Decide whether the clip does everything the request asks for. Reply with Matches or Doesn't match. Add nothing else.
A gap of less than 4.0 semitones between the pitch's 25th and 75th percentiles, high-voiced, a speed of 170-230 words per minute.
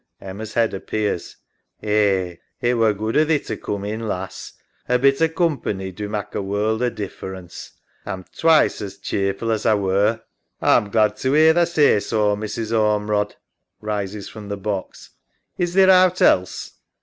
Doesn't match